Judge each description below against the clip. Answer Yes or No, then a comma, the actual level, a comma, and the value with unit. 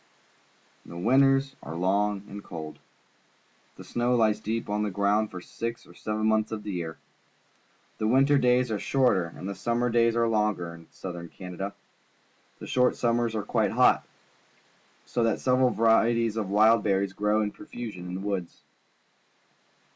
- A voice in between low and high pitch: No, low, 110 Hz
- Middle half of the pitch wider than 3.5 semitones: No, average, 3.2 semitones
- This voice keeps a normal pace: Yes, average, 170 wpm